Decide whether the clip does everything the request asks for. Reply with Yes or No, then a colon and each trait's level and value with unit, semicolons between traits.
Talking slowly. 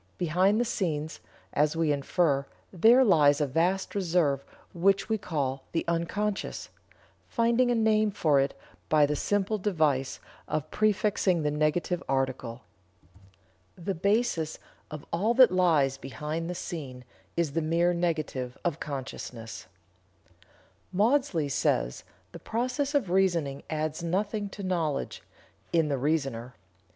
Yes: slow, 130 wpm